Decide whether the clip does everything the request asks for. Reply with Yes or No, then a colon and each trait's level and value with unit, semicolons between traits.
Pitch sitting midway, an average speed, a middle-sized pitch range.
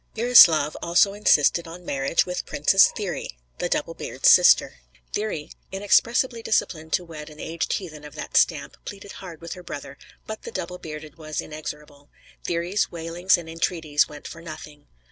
Yes: medium, 165 Hz; average, 165 wpm; average, 3.3 semitones